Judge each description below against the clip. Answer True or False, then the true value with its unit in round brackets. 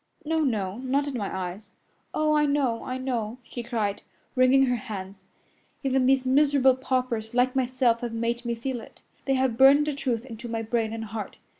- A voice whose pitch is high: True (250 Hz)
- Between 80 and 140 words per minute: False (190 wpm)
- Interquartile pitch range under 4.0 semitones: True (2.9 semitones)